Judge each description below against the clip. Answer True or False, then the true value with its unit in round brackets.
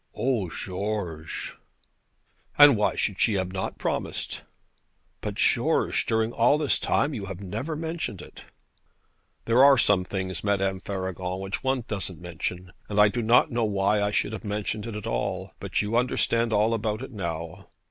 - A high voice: False (105 Hz)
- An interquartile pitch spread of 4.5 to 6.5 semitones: False (3.6 semitones)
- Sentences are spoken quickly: False (170 wpm)